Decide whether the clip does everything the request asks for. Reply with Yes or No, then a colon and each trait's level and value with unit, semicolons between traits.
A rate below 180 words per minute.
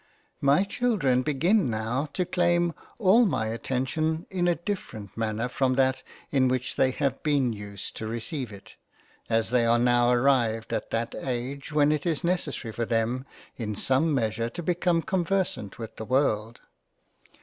Yes: average, 160 wpm